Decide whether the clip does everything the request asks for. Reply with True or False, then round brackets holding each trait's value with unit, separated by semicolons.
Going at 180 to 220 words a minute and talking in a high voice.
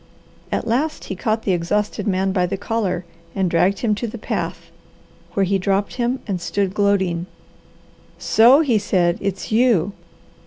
False (160 wpm; 200 Hz)